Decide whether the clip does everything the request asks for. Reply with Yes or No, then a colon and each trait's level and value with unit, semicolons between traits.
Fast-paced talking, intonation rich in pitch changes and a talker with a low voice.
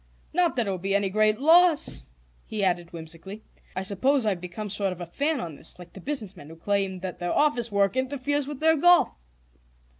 No: fast, 210 wpm; wide, 7.4 semitones; high, 205 Hz